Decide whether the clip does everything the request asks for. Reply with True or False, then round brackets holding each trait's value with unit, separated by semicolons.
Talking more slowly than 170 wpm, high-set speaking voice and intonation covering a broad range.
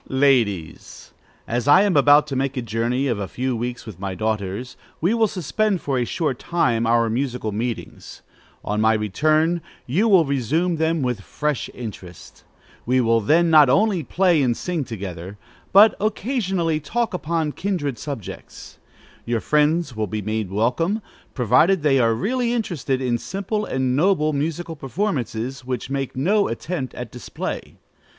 False (160 wpm; 135 Hz; 6.5 semitones)